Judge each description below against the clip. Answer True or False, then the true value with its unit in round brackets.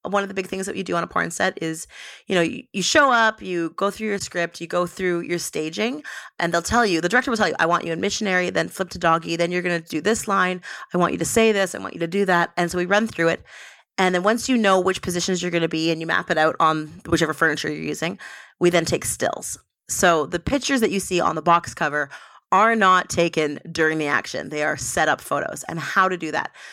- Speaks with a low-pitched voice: False (175 Hz)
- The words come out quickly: True (275 wpm)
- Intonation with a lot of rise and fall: False (2.7 semitones)